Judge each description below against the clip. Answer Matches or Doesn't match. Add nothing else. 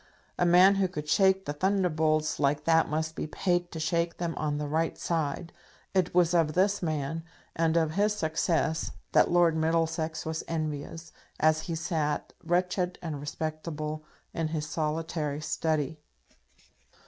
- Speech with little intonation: Matches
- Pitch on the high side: Doesn't match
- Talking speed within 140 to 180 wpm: Matches